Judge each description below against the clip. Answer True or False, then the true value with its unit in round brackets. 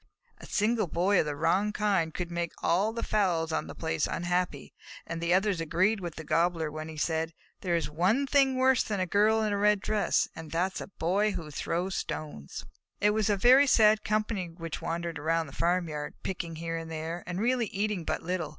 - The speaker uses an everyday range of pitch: True (4.2 semitones)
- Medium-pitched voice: True (180 Hz)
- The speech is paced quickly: True (215 wpm)